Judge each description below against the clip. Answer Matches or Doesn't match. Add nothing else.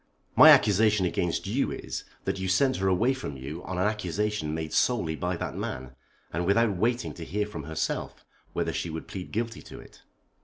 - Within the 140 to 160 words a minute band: Doesn't match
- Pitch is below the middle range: Matches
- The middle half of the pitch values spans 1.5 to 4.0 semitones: Doesn't match